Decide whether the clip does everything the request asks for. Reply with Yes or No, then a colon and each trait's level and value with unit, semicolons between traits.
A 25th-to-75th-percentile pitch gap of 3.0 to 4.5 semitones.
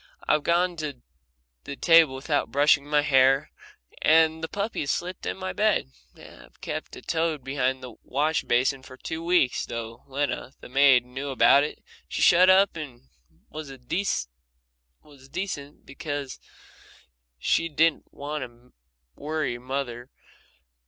Yes: average, 3.8 semitones